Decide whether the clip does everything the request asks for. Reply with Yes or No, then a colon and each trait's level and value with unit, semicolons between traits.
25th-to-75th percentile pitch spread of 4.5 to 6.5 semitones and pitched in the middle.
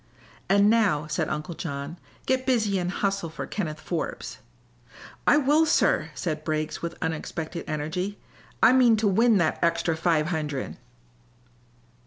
Yes: average, 4.9 semitones; medium, 170 Hz